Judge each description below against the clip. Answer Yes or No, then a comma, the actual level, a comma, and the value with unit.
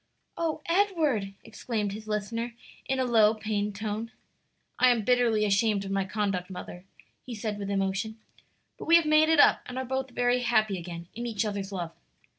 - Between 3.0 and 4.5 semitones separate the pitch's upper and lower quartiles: Yes, average, 3.7 semitones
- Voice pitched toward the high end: Yes, high, 220 Hz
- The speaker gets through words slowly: No, average, 185 wpm